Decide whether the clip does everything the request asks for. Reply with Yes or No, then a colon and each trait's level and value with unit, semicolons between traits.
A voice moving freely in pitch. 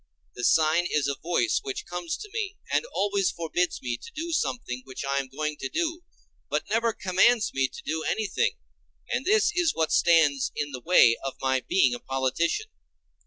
Yes: wide, 8.9 semitones